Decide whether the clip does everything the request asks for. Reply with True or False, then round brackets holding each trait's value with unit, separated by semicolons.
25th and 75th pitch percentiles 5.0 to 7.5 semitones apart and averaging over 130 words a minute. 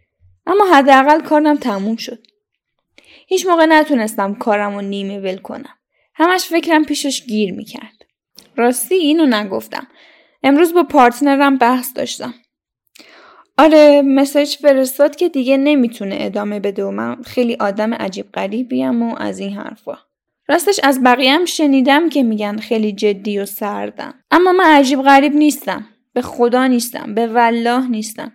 True (5.3 semitones; 140 wpm)